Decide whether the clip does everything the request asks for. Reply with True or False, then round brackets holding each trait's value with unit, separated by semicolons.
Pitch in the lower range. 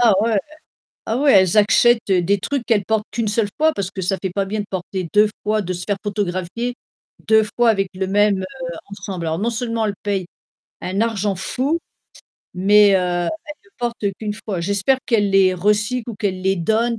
False (205 Hz)